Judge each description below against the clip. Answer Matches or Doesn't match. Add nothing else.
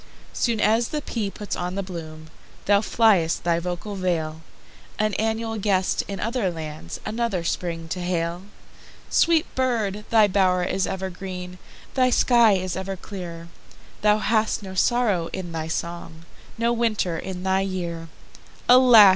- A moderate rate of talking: Doesn't match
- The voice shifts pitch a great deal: Doesn't match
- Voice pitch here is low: Doesn't match